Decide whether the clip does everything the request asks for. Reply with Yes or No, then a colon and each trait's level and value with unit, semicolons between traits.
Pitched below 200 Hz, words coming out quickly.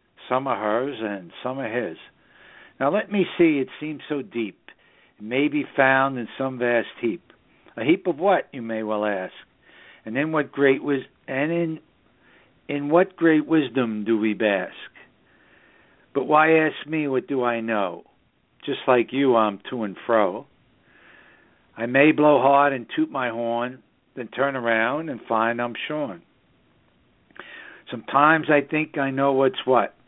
No: low, 135 Hz; average, 165 wpm